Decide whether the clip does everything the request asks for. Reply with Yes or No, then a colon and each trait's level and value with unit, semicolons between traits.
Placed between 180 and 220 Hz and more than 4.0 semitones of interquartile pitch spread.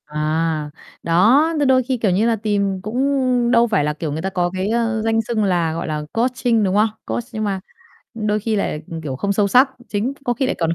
Yes: high, 210 Hz; average, 5.2 semitones